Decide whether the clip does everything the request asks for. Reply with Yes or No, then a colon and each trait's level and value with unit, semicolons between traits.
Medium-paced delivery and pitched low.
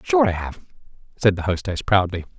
Yes: average, 175 wpm; very low, 95 Hz